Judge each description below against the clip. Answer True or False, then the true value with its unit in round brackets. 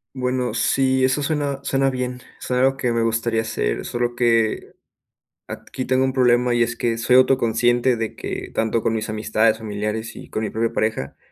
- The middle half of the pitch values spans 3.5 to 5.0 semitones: False (2.5 semitones)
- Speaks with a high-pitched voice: False (120 Hz)